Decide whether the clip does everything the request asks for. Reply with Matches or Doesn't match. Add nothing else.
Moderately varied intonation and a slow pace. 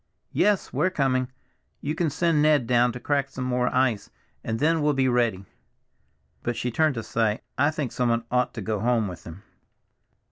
Doesn't match